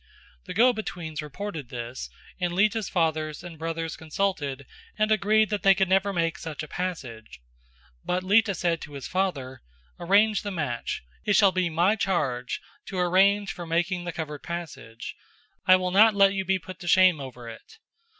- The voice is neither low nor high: Yes, medium, 180 Hz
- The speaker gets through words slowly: No, average, 175 wpm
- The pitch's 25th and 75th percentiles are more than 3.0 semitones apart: Yes, average, 4.0 semitones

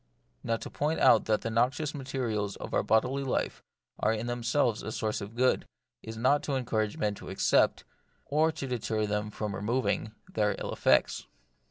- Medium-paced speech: Yes, average, 180 wpm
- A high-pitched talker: No, low, 115 Hz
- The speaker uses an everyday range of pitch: Yes, average, 3.5 semitones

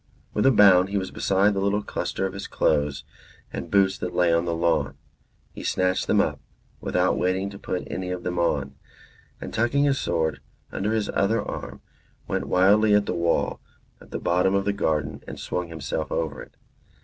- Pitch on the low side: Yes, very low, 95 Hz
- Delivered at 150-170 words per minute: No, average, 195 wpm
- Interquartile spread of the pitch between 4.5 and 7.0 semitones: No, average, 3.0 semitones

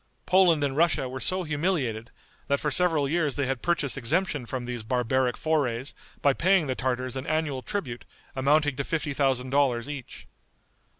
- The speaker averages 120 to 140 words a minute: No, average, 170 wpm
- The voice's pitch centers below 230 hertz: Yes, medium, 140 Hz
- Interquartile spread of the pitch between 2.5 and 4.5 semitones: Yes, average, 3.5 semitones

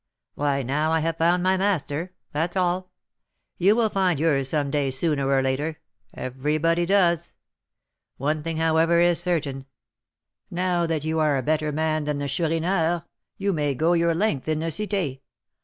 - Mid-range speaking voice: Yes, medium, 160 Hz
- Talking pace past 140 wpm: Yes, average, 165 wpm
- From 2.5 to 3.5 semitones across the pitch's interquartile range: Yes, average, 3.0 semitones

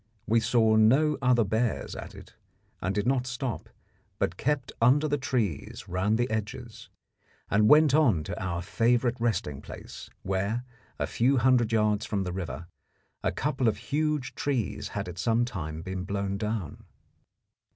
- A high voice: No, low, 110 Hz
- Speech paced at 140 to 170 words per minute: Yes, average, 160 wpm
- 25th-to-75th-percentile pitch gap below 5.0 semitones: Yes, average, 4.3 semitones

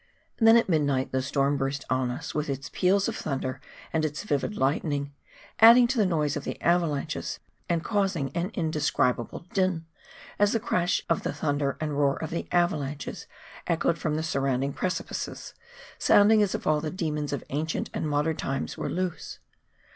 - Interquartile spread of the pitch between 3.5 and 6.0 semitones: Yes, average, 4.0 semitones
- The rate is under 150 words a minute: No, average, 175 wpm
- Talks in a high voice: No, medium, 155 Hz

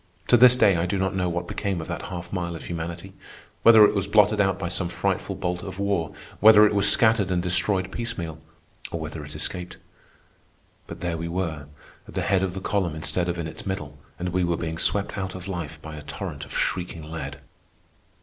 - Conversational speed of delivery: No, fast, 215 wpm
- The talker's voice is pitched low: Yes, very low, 90 Hz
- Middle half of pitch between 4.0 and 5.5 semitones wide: No, average, 2.8 semitones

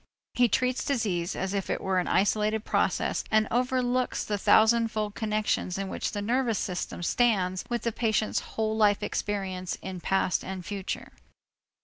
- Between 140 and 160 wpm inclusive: Yes, average, 155 wpm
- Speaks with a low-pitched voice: No, high, 210 Hz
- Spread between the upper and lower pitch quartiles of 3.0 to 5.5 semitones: Yes, average, 3.3 semitones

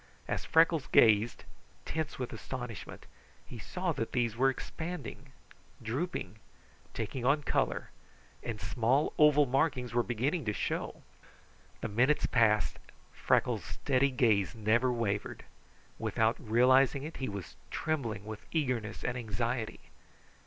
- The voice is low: Yes, low, 125 Hz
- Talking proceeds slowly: Yes, slow, 125 wpm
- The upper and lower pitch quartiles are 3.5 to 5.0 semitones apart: Yes, average, 3.8 semitones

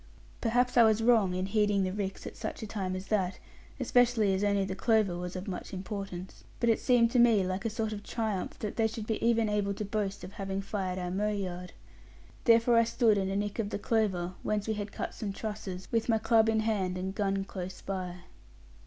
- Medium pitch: No, high, 205 Hz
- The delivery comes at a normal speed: No, fast, 225 wpm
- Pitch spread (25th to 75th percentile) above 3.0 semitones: No, average, 2.7 semitones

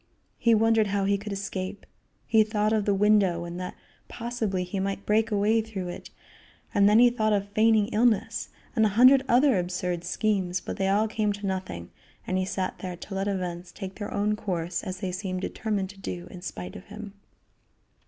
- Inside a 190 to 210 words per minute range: Yes, average, 200 wpm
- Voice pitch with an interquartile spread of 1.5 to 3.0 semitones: Yes, average, 2.7 semitones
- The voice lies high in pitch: Yes, high, 200 Hz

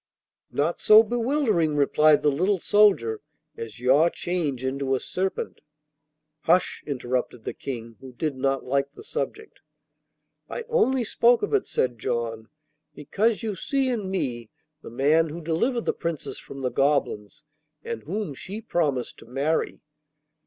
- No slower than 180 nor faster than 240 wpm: No, average, 145 wpm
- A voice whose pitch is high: No, medium, 150 Hz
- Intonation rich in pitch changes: Yes, wide, 7.8 semitones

